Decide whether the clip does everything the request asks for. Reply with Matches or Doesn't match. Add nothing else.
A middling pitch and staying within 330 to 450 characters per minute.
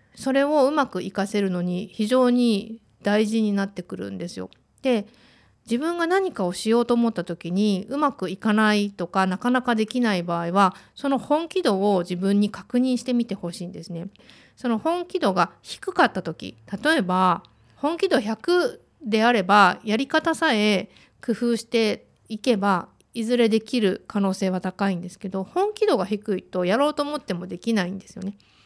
Doesn't match